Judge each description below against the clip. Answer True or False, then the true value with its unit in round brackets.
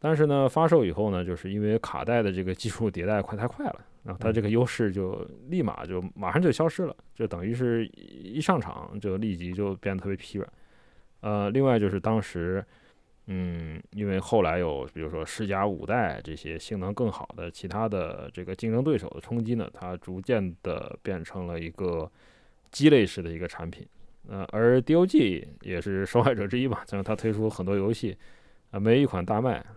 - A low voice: True (100 Hz)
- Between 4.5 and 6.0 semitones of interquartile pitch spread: False (4.0 semitones)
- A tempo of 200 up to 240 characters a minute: False (290 characters per minute)